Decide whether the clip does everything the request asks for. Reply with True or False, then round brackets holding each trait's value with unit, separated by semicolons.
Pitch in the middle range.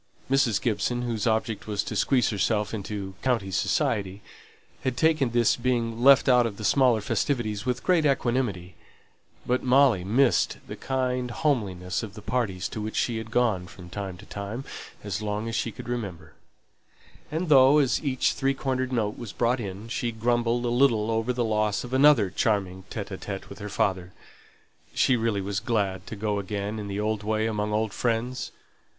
False (115 Hz)